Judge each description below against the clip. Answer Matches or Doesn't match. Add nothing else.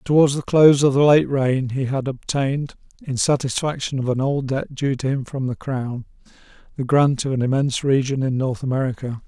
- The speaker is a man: Matches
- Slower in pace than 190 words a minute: Doesn't match